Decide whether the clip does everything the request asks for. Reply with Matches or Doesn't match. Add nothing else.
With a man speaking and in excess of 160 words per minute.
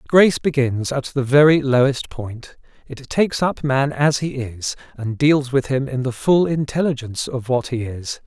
Matches